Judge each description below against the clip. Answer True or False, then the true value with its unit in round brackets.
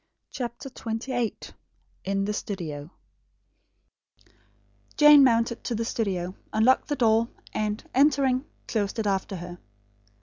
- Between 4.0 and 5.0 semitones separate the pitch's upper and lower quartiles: True (4.3 semitones)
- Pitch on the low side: False (225 Hz)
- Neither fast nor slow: False (110 wpm)